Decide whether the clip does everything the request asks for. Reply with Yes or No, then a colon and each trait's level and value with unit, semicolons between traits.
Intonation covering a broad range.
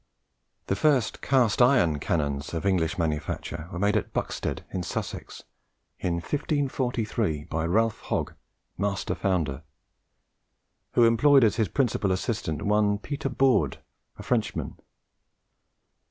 Yes: wide, 6.6 semitones